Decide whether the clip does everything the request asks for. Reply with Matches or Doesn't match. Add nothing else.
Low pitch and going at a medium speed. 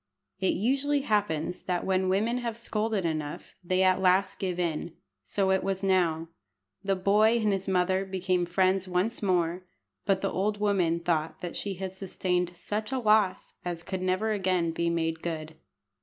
Doesn't match